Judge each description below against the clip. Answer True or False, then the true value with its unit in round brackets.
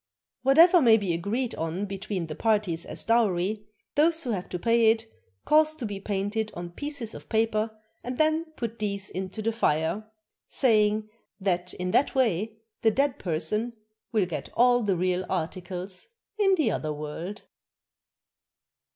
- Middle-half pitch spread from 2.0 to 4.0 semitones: False (4.6 semitones)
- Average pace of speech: True (155 wpm)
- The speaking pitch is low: False (215 Hz)